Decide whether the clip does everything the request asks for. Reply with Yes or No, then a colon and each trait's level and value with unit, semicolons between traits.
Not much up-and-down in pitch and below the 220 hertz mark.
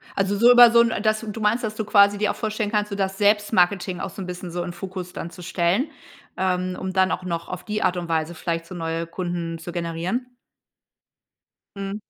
No: average, 3.3 semitones; high, 190 Hz